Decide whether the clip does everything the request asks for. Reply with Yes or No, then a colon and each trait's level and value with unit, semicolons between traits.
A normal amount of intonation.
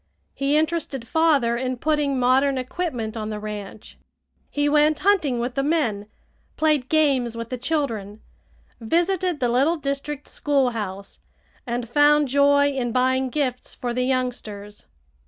Yes: average, 3.8 semitones